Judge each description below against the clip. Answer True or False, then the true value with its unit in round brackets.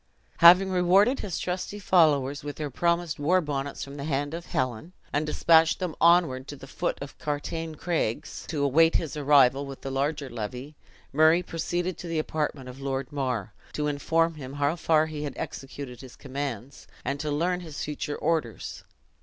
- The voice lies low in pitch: False (150 Hz)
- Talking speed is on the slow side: False (180 wpm)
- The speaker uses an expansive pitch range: False (3.3 semitones)